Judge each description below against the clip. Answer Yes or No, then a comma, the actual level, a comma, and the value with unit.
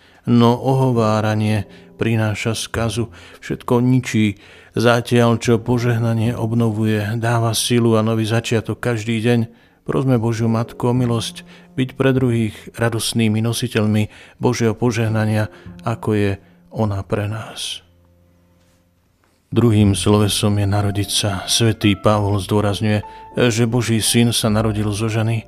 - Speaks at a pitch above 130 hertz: No, low, 110 Hz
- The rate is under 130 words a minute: Yes, average, 115 wpm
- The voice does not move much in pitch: Yes, narrow, 2.1 semitones